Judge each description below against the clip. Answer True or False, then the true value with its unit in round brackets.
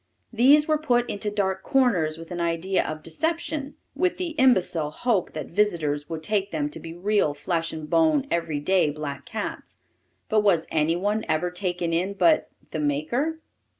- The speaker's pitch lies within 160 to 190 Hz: True (185 Hz)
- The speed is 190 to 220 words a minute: False (170 wpm)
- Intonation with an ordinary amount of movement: False (7.2 semitones)